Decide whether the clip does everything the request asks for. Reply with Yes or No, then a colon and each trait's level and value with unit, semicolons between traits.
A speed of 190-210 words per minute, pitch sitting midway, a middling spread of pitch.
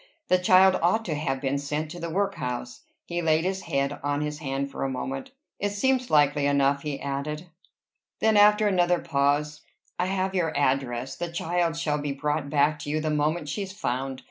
Yes: average, 195 wpm; medium, 150 Hz; average, 4.0 semitones